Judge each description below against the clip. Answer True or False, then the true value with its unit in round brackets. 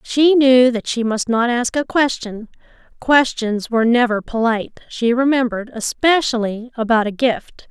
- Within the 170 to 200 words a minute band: False (150 wpm)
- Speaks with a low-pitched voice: False (240 Hz)